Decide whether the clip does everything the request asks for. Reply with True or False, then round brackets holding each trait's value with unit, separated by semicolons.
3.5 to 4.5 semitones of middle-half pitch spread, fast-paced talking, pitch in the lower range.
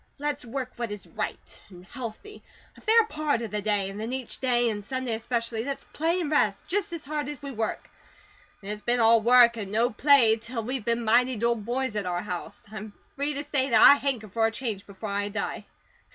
False (4.1 semitones; 220 wpm; 235 Hz)